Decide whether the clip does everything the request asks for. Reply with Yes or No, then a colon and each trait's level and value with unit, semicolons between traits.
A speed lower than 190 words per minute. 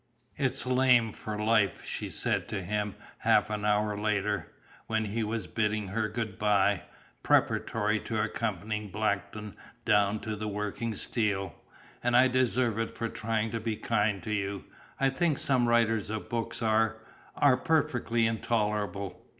Yes: average, 150 wpm